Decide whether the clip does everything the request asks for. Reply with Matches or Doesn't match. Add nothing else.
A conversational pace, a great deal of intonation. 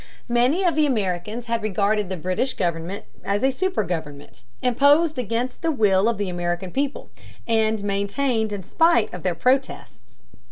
Matches